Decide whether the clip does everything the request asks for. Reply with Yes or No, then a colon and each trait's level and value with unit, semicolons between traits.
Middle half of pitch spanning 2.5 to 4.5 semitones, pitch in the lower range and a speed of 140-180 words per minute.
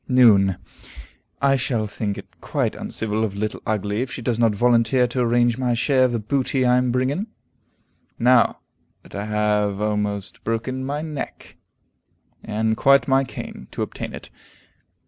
Yes: average, 3.4 semitones; low, 120 Hz; average, 160 wpm